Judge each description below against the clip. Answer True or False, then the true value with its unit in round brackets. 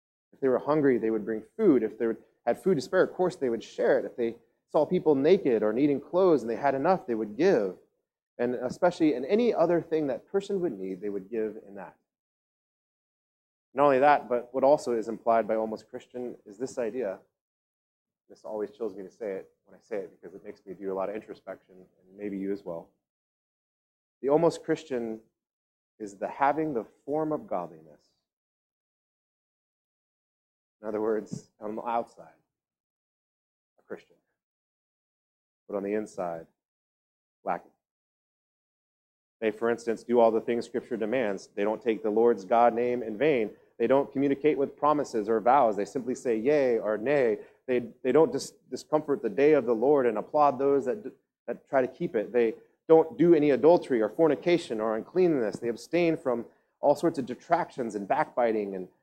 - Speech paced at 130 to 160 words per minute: False (185 wpm)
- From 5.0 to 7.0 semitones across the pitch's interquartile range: True (5.4 semitones)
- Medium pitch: False (125 Hz)